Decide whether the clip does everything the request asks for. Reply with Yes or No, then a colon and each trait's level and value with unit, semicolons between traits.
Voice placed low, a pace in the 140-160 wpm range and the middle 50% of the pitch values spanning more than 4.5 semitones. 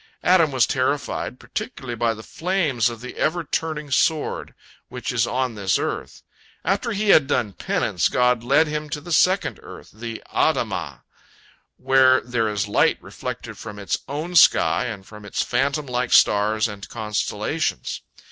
Yes: low, 125 Hz; average, 155 wpm; average, 5.2 semitones